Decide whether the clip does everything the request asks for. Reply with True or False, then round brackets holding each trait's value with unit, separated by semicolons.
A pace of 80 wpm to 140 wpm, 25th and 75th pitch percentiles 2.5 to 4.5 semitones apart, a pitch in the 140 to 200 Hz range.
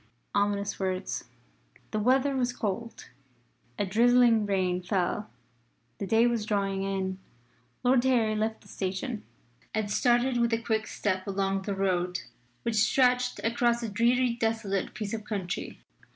False (135 wpm; 3.4 semitones; 215 Hz)